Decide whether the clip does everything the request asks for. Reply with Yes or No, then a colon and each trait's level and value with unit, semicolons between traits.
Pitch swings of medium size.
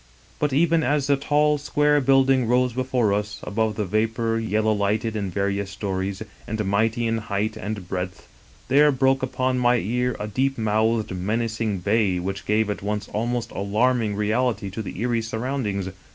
Yes: average, 3.7 semitones